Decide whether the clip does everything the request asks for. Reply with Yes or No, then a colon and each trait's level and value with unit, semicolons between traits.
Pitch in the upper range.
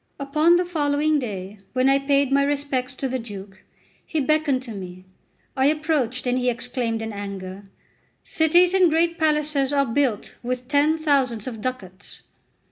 Yes: very high, 270 Hz